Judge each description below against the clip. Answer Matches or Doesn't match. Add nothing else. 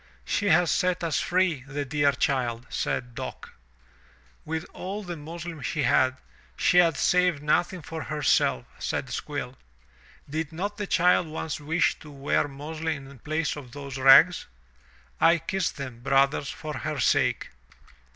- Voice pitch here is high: Doesn't match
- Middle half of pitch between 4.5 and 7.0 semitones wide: Doesn't match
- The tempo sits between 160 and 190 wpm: Doesn't match